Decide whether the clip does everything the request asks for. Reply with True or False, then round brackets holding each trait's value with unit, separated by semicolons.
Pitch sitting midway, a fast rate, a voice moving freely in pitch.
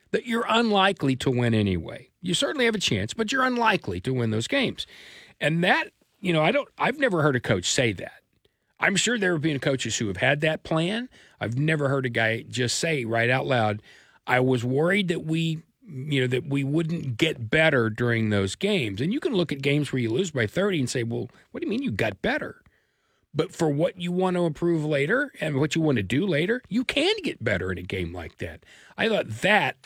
True (150 Hz; 230 wpm; 6.7 semitones)